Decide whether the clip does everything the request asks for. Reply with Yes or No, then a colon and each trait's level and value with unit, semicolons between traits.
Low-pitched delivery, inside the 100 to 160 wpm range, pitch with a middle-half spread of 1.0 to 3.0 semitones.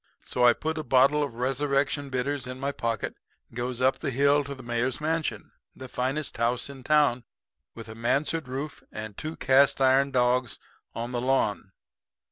No: low, 130 Hz; average, 185 wpm; narrow, 2.5 semitones